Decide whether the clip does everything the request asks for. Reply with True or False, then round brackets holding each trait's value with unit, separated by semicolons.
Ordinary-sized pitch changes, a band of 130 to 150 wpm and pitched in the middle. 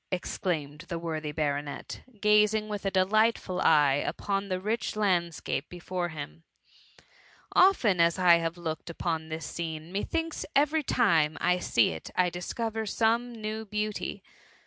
True (4.7 semitones; 145 wpm; 180 Hz)